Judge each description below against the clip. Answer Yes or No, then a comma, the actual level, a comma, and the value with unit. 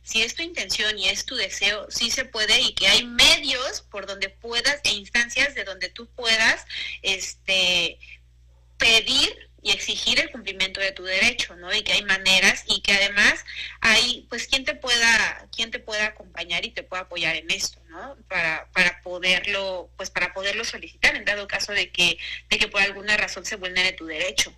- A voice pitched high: Yes, high, 200 Hz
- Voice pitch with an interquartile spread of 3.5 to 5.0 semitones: Yes, average, 3.8 semitones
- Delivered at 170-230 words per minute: Yes, fast, 190 wpm